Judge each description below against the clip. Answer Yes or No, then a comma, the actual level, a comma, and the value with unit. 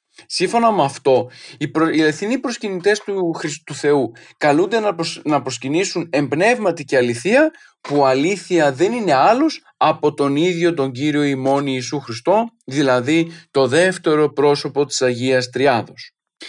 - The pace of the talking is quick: No, average, 125 wpm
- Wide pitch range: No, average, 5.0 semitones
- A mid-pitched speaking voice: Yes, medium, 155 Hz